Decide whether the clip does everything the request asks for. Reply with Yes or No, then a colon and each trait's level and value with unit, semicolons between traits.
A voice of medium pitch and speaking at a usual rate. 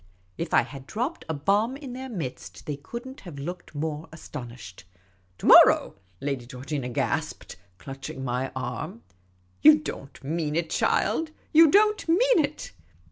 Yes: medium, 150 Hz; average, 175 wpm